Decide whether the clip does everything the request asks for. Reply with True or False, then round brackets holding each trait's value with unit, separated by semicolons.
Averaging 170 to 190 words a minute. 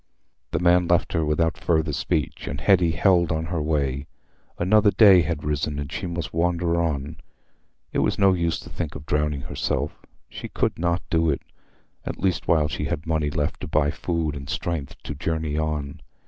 True (185 wpm)